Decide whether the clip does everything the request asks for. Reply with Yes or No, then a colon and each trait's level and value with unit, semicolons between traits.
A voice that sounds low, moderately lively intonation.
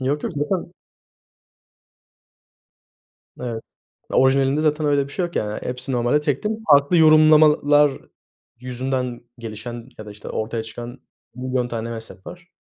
Yes: low, 130 Hz; average, 3.9 semitones